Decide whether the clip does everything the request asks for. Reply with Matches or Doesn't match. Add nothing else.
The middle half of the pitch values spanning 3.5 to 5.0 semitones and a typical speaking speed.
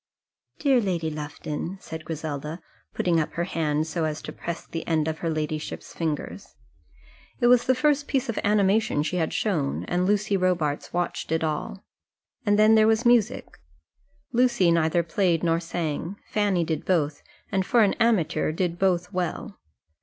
Matches